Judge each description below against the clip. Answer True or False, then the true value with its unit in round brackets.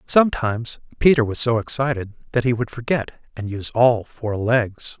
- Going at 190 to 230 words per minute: False (170 wpm)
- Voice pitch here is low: True (120 Hz)